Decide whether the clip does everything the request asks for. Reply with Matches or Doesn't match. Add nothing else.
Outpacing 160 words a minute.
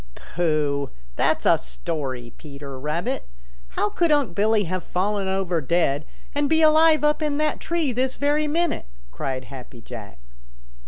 Doesn't match